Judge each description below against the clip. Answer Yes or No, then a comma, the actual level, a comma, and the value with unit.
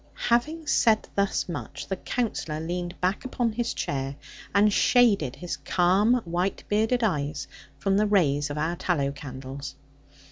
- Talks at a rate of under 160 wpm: Yes, average, 145 wpm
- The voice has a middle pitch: Yes, medium, 180 Hz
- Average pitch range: No, wide, 6.6 semitones